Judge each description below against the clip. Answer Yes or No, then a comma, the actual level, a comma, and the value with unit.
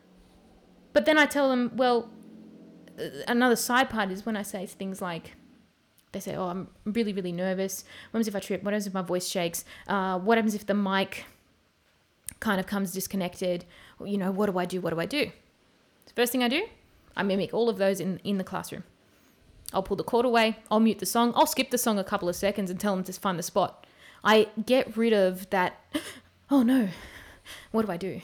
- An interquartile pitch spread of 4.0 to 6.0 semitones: No, average, 3.6 semitones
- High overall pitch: Yes, high, 200 Hz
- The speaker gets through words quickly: Yes, fast, 220 wpm